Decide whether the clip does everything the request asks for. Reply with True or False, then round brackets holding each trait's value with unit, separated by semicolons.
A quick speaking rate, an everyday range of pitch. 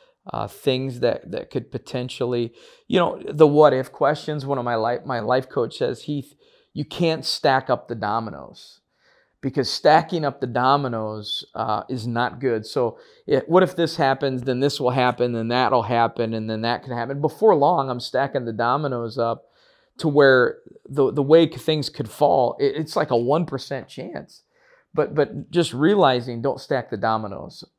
False (180 wpm; 4.1 semitones)